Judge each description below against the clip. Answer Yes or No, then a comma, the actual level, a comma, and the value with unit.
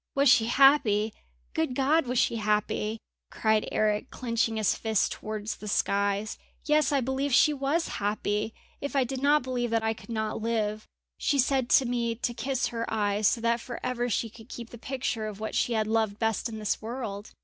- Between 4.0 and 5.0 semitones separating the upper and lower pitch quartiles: No, average, 3.1 semitones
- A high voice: Yes, high, 230 Hz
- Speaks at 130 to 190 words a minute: No, average, 200 wpm